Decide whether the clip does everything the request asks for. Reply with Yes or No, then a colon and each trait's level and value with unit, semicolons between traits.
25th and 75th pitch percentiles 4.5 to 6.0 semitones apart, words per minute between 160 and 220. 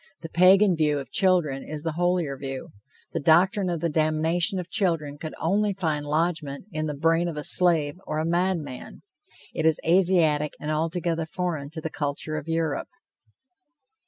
No: average, 2.7 semitones; average, 170 wpm